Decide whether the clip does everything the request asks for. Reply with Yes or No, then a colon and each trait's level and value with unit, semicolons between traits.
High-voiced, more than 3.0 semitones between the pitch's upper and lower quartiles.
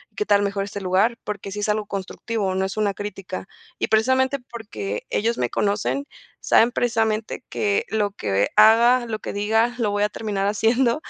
No: high, 210 Hz; narrow, 2.5 semitones